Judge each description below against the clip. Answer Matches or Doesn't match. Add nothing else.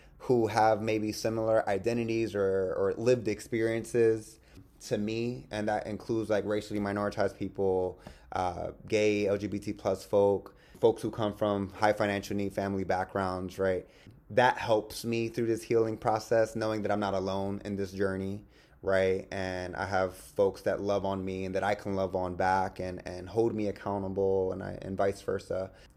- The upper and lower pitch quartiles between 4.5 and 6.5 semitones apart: Doesn't match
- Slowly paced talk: Doesn't match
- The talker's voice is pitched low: Matches